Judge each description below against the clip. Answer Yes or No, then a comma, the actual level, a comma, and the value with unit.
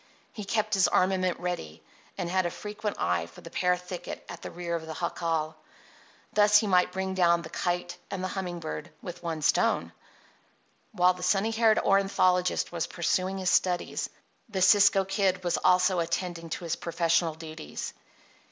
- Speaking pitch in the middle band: Yes, medium, 180 Hz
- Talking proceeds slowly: No, average, 170 wpm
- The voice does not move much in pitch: Yes, narrow, 2.0 semitones